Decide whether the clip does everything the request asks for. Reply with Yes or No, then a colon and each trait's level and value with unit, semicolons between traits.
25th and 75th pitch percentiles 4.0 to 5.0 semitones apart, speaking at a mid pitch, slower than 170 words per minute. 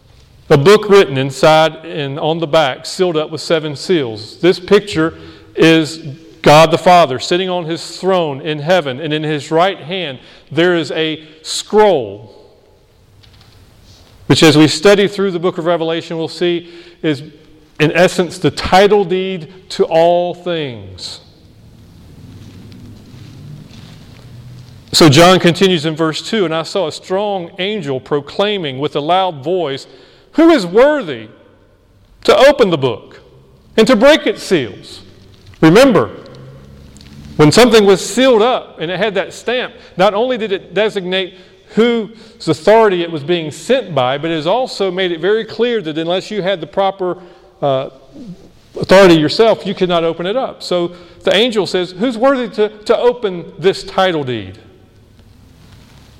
Yes: average, 4.7 semitones; medium, 170 Hz; average, 150 wpm